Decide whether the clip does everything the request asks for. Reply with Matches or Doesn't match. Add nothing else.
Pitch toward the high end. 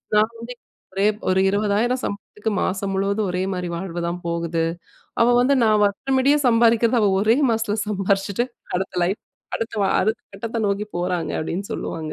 Matches